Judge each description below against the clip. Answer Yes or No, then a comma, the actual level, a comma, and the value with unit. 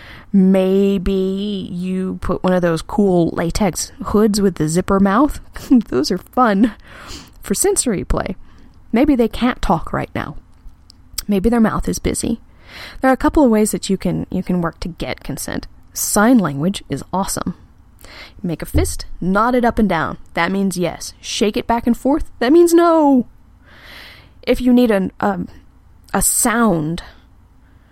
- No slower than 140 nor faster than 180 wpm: Yes, average, 160 wpm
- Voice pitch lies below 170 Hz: No, high, 195 Hz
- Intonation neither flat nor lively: No, wide, 5.9 semitones